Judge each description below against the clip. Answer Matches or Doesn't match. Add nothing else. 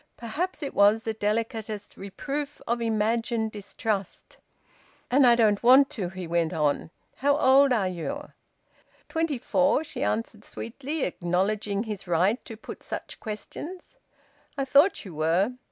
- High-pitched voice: Matches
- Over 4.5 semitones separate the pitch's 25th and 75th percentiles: Matches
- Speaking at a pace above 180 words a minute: Doesn't match